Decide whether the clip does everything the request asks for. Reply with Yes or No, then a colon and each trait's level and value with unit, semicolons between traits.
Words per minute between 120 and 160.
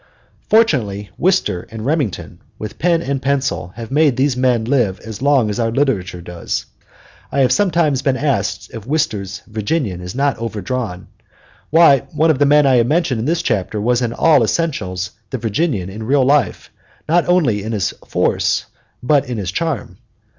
No: average, 175 wpm